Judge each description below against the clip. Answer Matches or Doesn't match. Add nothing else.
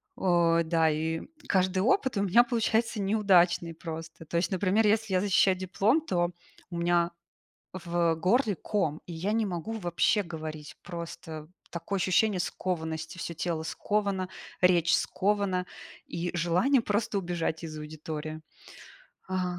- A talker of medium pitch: Matches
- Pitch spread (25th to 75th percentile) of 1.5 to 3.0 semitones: Doesn't match